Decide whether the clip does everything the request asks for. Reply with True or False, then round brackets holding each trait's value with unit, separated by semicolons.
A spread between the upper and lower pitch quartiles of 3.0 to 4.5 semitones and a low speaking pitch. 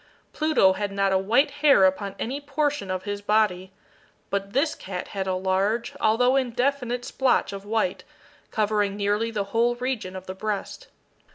False (4.1 semitones; 210 Hz)